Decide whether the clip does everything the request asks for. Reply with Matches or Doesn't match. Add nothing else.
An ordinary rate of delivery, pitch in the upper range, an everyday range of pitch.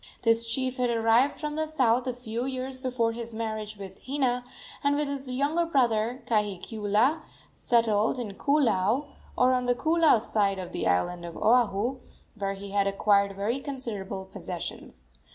Matches